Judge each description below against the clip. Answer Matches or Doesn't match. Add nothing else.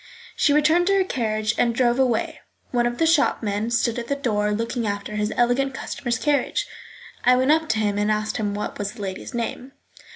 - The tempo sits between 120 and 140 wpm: Doesn't match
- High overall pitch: Matches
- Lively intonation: Doesn't match